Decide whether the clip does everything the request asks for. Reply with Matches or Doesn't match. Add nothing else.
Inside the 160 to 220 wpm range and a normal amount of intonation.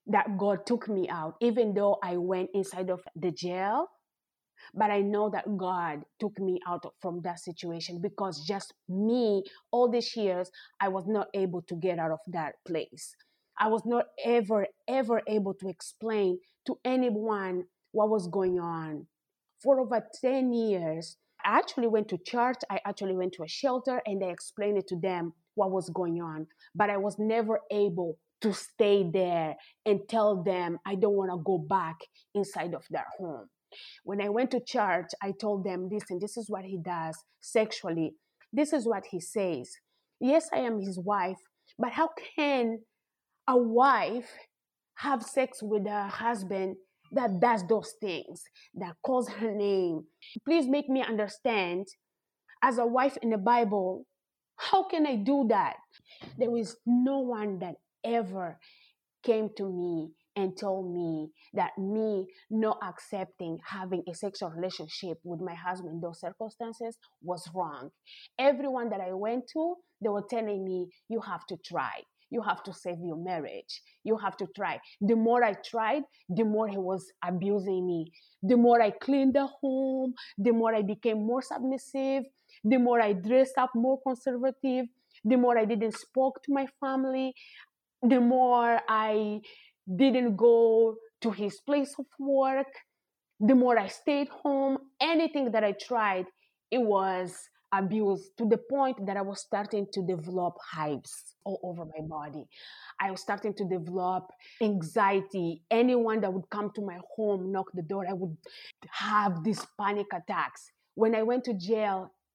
Matches